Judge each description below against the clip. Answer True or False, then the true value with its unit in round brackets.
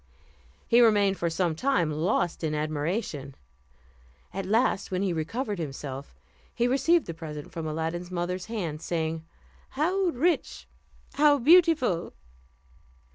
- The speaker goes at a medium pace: False (130 wpm)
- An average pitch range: False (7.3 semitones)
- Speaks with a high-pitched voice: False (180 Hz)